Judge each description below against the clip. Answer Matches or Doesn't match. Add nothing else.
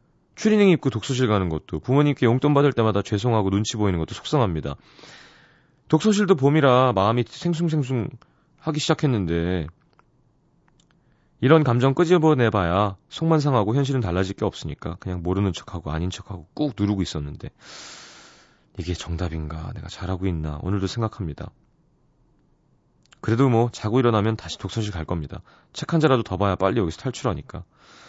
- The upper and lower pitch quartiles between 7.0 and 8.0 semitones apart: Matches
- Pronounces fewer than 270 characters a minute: Doesn't match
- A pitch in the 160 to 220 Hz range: Doesn't match